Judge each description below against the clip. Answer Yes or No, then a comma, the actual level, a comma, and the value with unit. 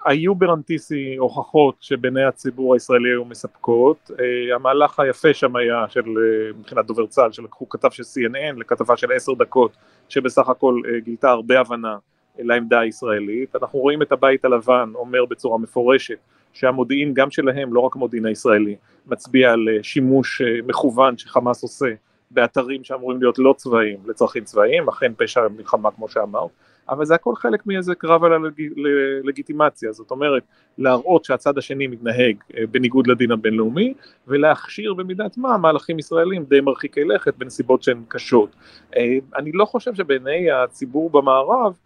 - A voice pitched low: Yes, low, 130 Hz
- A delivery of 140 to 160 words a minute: Yes, fast, 150 wpm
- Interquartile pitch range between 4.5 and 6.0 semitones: No, average, 3.8 semitones